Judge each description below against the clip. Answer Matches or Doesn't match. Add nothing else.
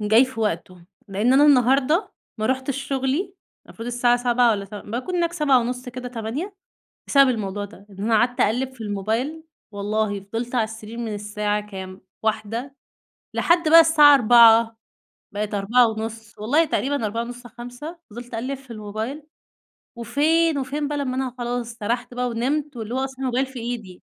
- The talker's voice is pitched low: Doesn't match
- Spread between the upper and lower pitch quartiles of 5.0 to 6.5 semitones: Doesn't match